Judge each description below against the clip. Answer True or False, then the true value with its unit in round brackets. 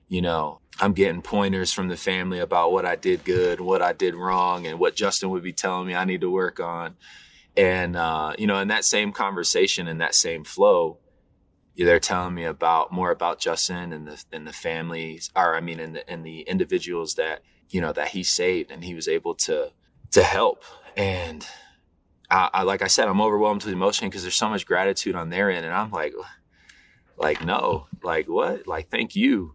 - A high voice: False (95 Hz)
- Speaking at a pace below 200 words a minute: False (205 wpm)